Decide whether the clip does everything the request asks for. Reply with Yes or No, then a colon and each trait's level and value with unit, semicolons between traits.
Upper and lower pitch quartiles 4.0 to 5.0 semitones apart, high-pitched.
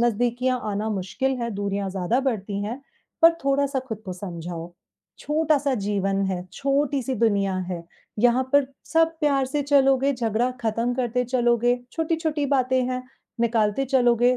Yes: average, 4.7 semitones; high, 245 Hz